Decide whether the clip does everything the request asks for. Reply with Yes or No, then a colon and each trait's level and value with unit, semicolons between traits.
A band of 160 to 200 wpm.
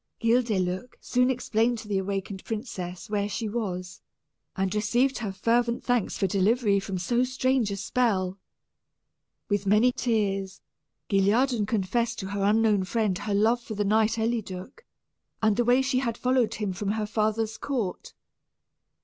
No: average, 150 wpm